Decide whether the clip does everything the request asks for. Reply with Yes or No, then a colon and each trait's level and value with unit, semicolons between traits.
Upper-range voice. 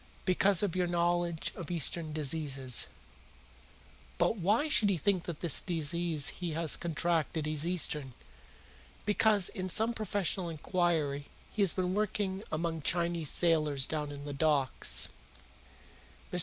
No: medium, 170 Hz